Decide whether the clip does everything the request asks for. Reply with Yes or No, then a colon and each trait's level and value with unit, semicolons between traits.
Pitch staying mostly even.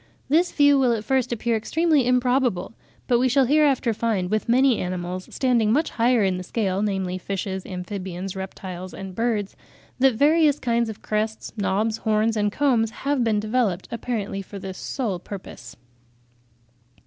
No: average, 4.6 semitones